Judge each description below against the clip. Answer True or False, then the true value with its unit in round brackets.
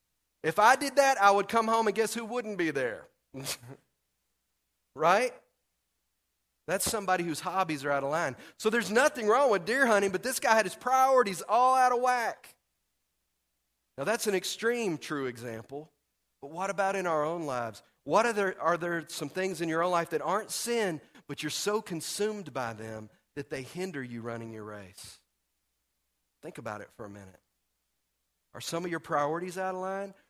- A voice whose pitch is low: False (165 Hz)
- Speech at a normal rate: True (185 wpm)